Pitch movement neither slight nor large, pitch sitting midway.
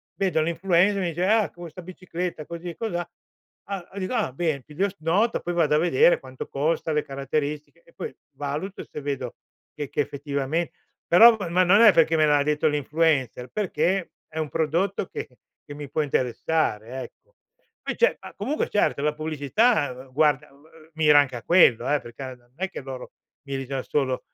Yes: average, 4.3 semitones; medium, 155 Hz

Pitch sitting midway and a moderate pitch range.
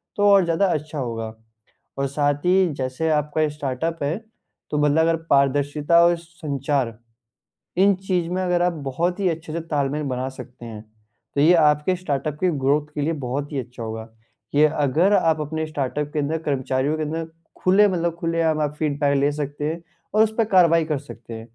Yes: medium, 150 Hz; average, 3.1 semitones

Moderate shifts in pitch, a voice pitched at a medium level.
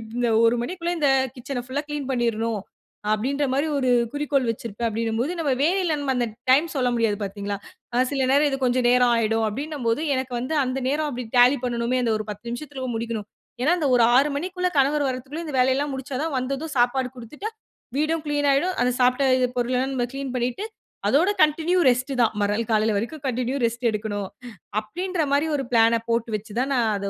No: average, 3.6 semitones; very high, 255 Hz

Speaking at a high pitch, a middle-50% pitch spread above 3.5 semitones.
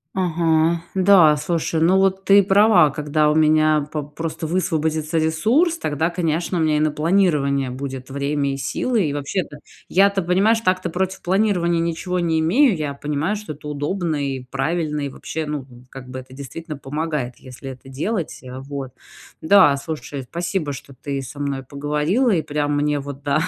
No: medium, 155 Hz; average, 3.9 semitones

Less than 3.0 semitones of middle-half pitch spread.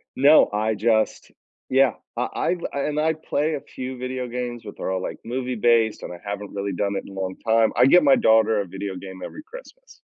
No: average, 5.0 semitones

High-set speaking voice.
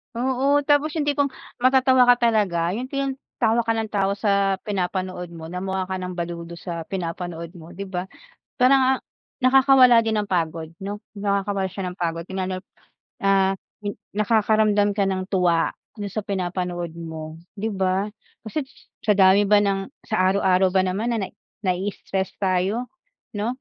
Yes: high, 195 Hz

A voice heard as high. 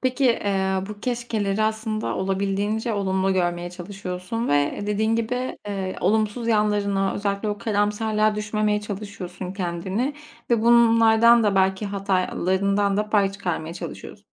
Yes: high, 205 Hz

